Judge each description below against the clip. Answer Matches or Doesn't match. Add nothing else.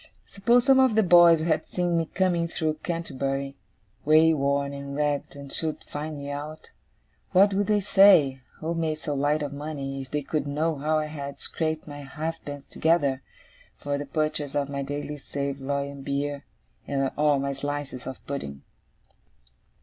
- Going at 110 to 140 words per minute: Doesn't match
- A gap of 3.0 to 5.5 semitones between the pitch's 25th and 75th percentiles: Doesn't match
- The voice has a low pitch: Doesn't match